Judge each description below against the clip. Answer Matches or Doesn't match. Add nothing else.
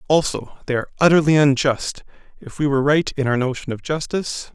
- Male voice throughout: Matches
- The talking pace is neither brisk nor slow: Matches